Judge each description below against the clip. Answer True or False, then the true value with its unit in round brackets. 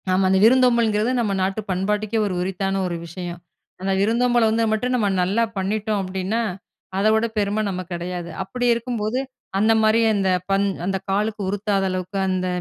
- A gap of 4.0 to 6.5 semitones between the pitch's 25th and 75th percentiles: False (2.7 semitones)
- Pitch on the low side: False (205 Hz)